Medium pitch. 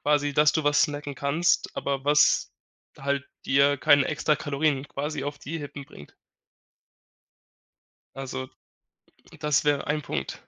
Yes: medium, 145 Hz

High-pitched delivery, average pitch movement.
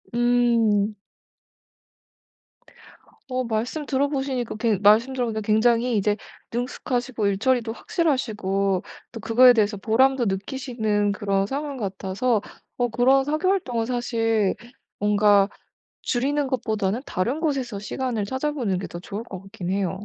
Yes: high, 230 Hz; average, 3.8 semitones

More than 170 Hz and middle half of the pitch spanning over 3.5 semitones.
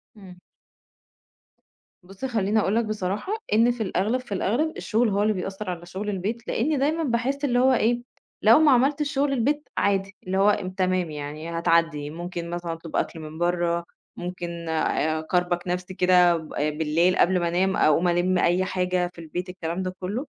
Yes: medium, 185 Hz; average, 4.5 semitones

